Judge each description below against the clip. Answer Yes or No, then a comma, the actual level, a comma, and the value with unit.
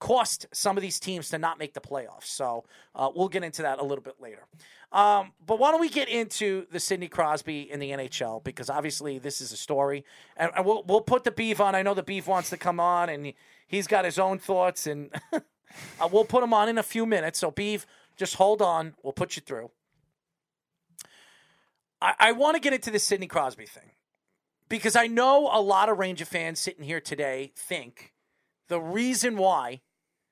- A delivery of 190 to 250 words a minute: Yes, fast, 205 wpm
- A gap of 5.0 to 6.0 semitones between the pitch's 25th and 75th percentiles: Yes, wide, 5.6 semitones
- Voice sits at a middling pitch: Yes, medium, 180 Hz